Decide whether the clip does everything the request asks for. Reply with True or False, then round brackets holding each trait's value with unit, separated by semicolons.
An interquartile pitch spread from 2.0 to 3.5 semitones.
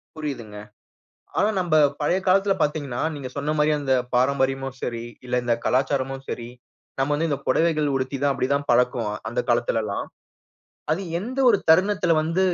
False (4.1 semitones)